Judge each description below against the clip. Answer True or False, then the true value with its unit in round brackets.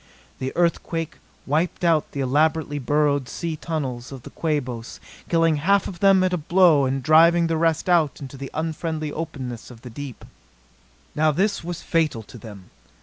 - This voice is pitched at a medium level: True (155 Hz)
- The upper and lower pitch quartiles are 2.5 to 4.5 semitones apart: True (3.6 semitones)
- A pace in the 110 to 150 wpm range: False (170 wpm)